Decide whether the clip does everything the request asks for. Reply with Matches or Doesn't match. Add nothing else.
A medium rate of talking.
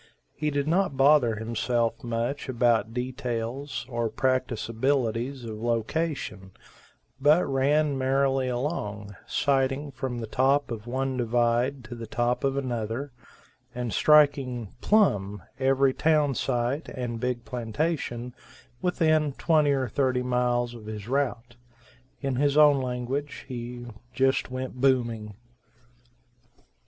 Doesn't match